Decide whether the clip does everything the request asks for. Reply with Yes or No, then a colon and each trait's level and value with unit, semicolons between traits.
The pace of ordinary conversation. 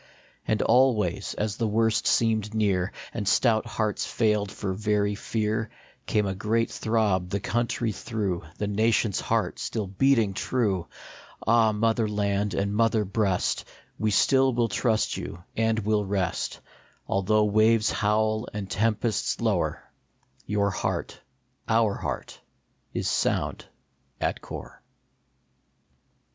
No: slow, 130 wpm